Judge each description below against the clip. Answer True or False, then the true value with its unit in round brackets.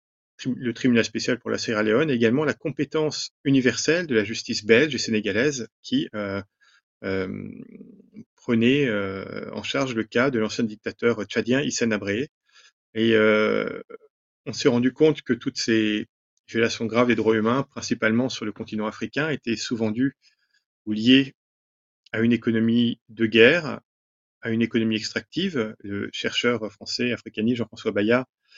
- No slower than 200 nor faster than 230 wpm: False (150 wpm)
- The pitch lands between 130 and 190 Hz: False (115 Hz)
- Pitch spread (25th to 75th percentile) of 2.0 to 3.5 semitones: True (3.1 semitones)